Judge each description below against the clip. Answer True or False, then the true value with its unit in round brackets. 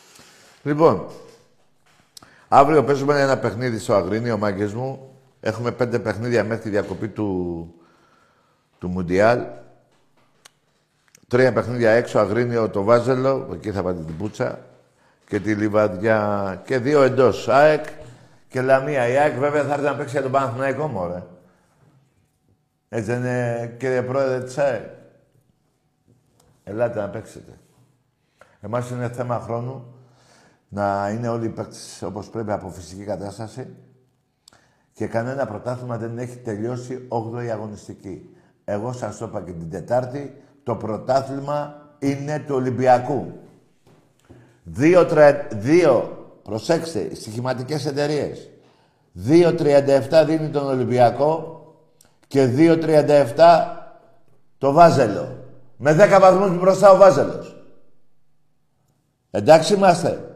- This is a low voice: True (125 Hz)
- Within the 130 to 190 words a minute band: False (115 wpm)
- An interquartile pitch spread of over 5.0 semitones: False (4.5 semitones)